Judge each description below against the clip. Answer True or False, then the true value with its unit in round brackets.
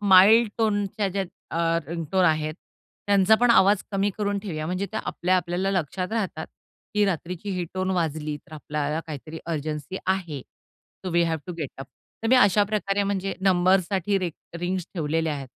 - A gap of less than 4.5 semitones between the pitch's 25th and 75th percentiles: True (3.7 semitones)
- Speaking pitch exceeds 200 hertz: False (185 Hz)